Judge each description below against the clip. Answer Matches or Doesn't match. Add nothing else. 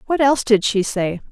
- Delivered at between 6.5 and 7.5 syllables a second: Doesn't match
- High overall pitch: Matches